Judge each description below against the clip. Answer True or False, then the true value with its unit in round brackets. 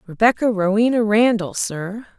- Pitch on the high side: True (210 Hz)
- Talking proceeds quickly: False (110 wpm)